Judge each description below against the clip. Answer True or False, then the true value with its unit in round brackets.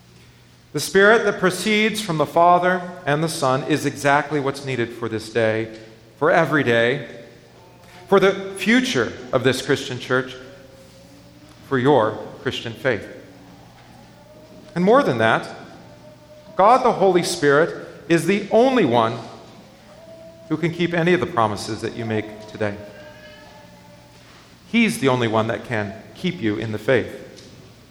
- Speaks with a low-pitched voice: True (130 Hz)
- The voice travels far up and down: True (7.5 semitones)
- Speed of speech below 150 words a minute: True (140 wpm)